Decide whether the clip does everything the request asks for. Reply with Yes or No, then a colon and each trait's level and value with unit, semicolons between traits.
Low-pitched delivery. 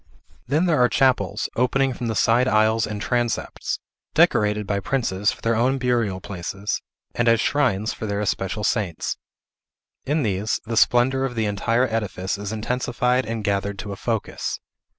Yes: low, 115 Hz